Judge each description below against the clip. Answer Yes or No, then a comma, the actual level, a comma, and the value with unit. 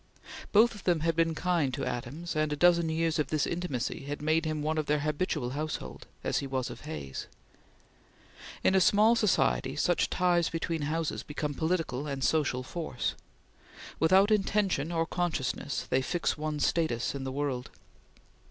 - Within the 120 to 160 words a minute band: No, average, 170 wpm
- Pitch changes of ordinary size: Yes, average, 3.4 semitones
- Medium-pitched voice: Yes, medium, 155 Hz